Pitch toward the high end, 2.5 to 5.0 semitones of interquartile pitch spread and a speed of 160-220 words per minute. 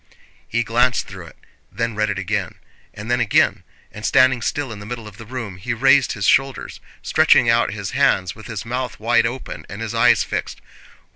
No: low, 115 Hz; average, 2.8 semitones; average, 200 wpm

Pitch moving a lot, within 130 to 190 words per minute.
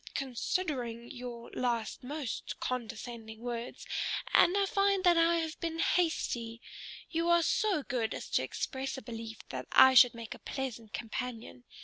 Yes: wide, 6.0 semitones; average, 150 wpm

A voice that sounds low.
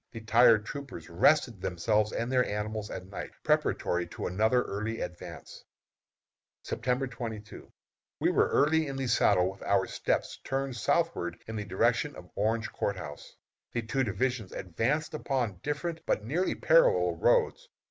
Yes: low, 115 Hz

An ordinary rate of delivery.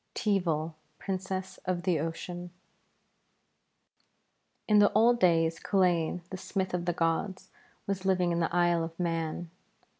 No: slow, 130 wpm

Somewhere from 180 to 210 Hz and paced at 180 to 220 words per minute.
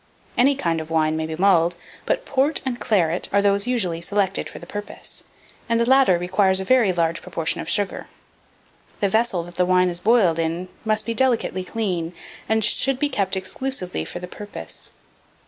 Yes: high, 190 Hz; average, 185 wpm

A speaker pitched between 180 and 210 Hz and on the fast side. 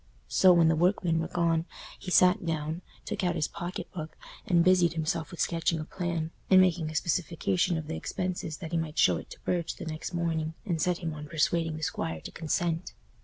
No: medium, 165 Hz; fast, 215 wpm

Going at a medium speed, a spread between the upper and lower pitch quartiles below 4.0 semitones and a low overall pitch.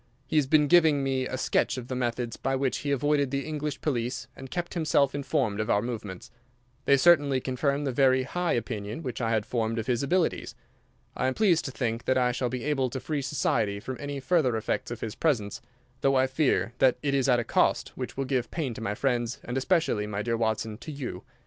No: fast, 225 wpm; average, 3.1 semitones; low, 130 Hz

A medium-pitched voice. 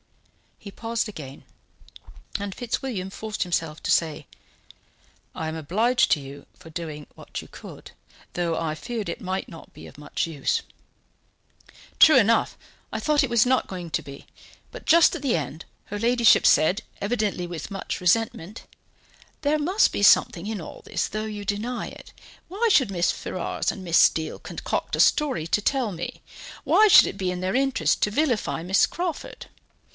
No: high, 200 Hz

